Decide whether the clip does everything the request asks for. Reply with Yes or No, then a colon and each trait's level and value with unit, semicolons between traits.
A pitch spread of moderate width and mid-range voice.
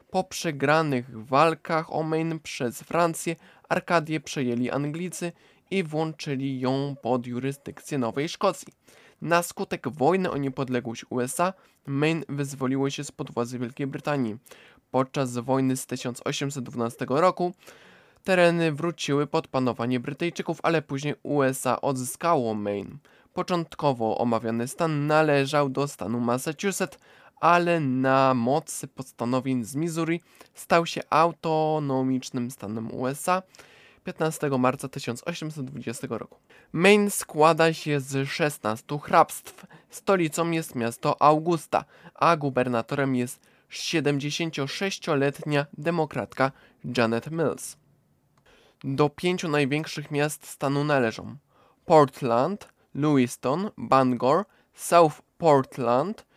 Yes: average, 4.1 semitones; medium, 145 Hz